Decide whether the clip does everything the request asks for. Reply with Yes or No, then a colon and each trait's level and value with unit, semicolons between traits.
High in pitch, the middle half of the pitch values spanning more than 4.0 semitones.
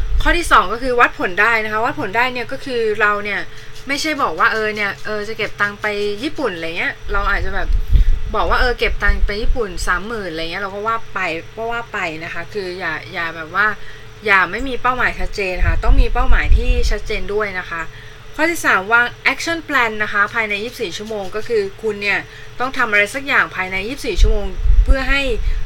No: high, 215 Hz; average, 3.4 semitones